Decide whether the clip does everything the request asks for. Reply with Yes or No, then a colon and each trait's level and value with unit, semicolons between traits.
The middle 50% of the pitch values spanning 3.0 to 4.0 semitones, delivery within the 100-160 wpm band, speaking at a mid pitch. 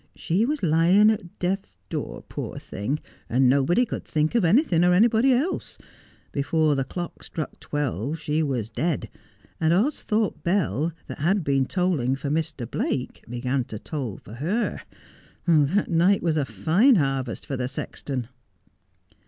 No: wide, 5.6 semitones; average, 155 wpm; medium, 160 Hz